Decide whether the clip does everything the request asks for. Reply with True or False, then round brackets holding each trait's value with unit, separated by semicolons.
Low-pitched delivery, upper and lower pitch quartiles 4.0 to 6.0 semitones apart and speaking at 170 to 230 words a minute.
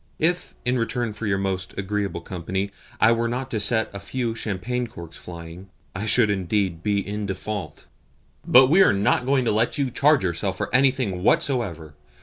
True (105 Hz; 4.4 semitones; 180 wpm)